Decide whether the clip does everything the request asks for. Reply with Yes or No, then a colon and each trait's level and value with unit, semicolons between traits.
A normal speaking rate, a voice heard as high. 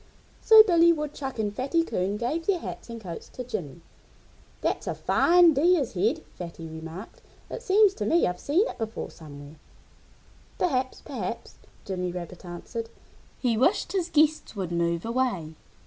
Yes: average, 155 wpm; high, 235 Hz